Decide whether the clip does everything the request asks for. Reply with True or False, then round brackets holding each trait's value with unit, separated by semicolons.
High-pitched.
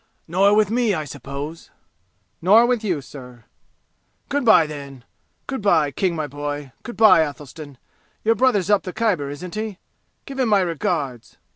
False (170 Hz)